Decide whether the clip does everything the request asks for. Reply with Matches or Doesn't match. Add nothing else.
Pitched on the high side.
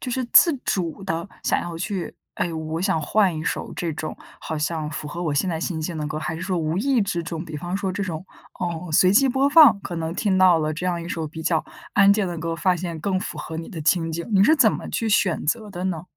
Doesn't match